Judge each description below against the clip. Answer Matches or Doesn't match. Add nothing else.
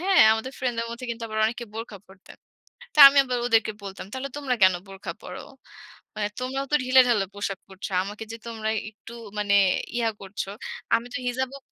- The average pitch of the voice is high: Matches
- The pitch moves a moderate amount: Matches